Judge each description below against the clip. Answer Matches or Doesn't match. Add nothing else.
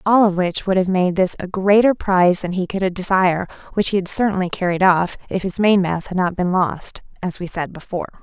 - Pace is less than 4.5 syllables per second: Doesn't match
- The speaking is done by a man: Doesn't match